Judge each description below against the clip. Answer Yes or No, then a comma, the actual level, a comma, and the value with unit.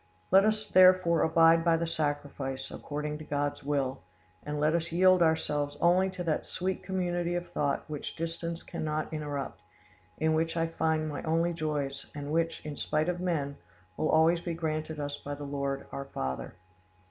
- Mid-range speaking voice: Yes, medium, 160 Hz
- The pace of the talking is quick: No, average, 175 wpm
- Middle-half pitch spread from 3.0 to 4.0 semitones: No, narrow, 2.6 semitones